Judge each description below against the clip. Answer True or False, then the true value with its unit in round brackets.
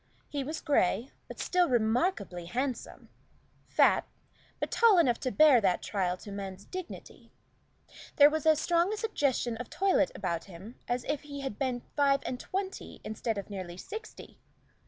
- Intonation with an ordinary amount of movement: False (7.4 semitones)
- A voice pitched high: True (260 Hz)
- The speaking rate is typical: True (160 wpm)